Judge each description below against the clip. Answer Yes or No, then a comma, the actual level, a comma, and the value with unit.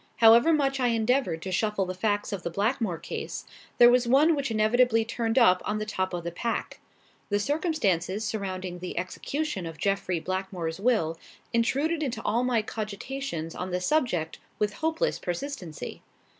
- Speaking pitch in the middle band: No, high, 215 Hz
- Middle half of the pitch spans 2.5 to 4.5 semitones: No, wide, 5.4 semitones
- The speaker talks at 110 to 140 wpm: No, average, 165 wpm